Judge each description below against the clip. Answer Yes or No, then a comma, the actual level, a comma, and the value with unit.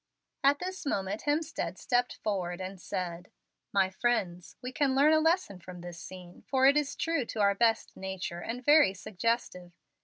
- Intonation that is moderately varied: No, wide, 7.1 semitones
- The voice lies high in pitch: Yes, high, 215 Hz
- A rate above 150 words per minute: Yes, average, 175 wpm